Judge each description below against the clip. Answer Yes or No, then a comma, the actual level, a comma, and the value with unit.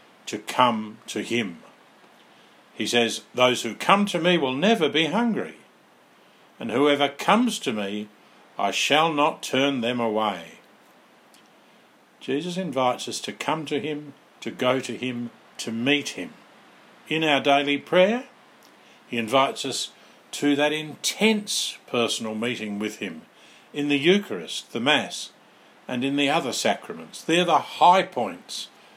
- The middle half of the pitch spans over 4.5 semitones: Yes, average, 5.1 semitones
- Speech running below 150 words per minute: Yes, average, 140 wpm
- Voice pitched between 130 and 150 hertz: Yes, medium, 140 Hz